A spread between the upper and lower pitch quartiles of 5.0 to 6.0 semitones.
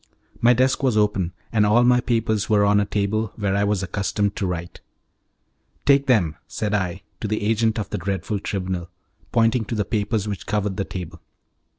No: narrow, 2.4 semitones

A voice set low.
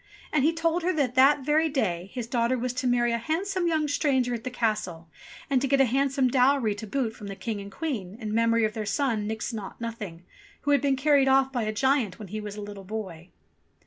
No: high, 240 Hz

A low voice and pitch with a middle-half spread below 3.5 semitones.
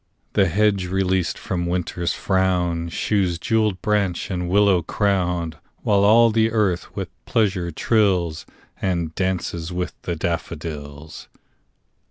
Yes: very low, 90 Hz; average, 2.9 semitones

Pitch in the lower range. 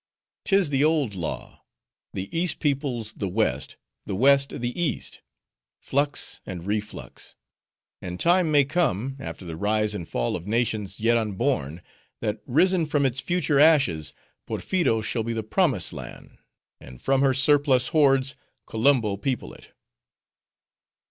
Yes: low, 125 Hz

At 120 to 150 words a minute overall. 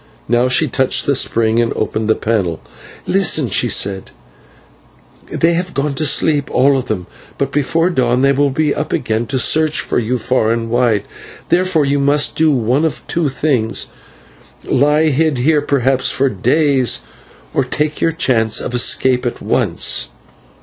No: average, 165 wpm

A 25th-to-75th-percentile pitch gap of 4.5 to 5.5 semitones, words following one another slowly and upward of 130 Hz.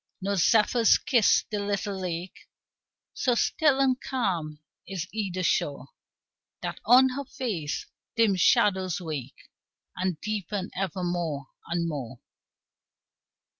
Yes: average, 4.8 semitones; slow, 115 wpm; high, 190 Hz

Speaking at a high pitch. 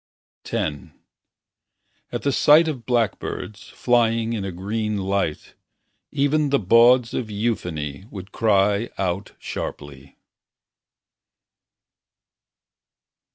No: low, 110 Hz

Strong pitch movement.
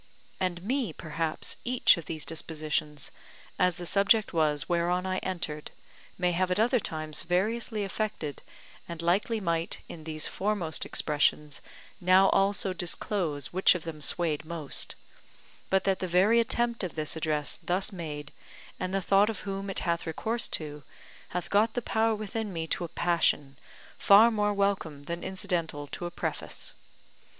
No: average, 3.9 semitones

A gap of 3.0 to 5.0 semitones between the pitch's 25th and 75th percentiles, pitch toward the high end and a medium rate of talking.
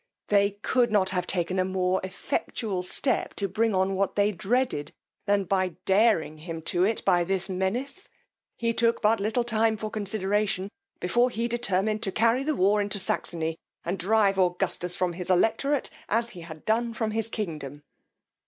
Yes: average, 3.5 semitones; high, 200 Hz; average, 170 wpm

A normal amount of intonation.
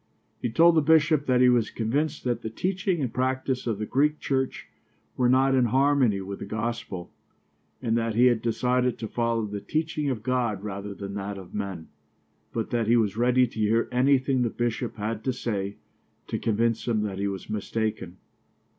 Yes: average, 3.5 semitones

